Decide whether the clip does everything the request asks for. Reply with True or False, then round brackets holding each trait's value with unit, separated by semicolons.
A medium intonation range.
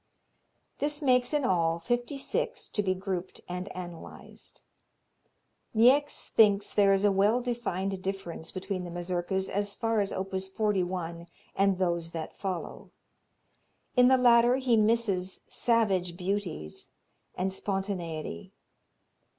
True (4.1 semitones)